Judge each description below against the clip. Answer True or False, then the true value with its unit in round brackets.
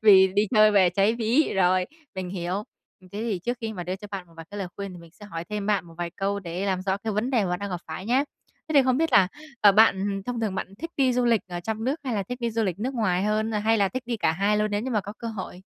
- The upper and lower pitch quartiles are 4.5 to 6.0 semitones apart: False (3.3 semitones)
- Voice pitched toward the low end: False (205 Hz)